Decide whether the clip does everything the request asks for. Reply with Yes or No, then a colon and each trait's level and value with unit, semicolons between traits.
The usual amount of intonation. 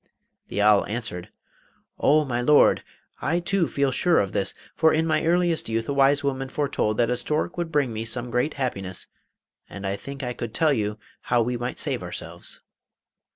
Yes: average, 4.9 semitones